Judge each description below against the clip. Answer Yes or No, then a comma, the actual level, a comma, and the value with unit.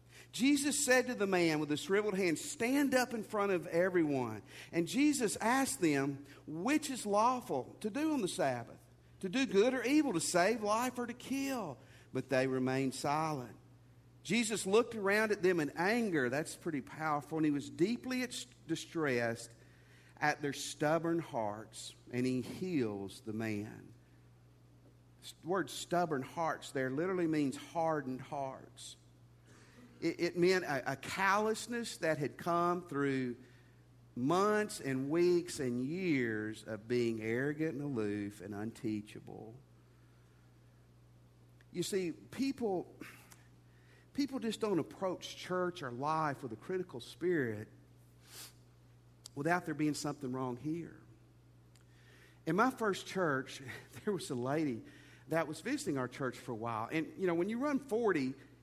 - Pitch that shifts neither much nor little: No, wide, 7.6 semitones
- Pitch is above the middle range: No, medium, 145 Hz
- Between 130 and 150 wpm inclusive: Yes, average, 145 wpm